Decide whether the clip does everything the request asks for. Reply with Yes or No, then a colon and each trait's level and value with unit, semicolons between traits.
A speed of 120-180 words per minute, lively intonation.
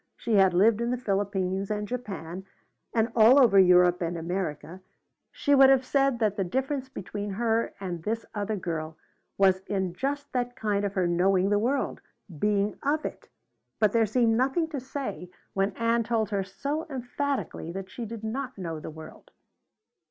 No: average, 175 wpm; average, 4.7 semitones